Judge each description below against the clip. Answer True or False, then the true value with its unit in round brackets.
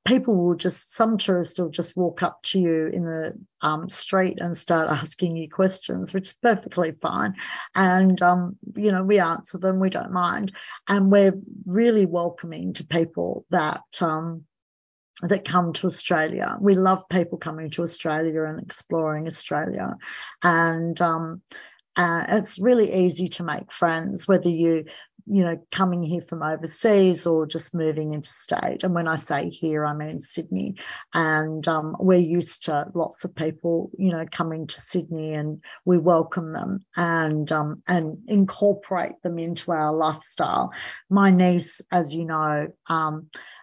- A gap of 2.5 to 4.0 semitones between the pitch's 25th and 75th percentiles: True (2.8 semitones)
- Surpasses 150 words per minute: True (160 wpm)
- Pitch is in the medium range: True (175 Hz)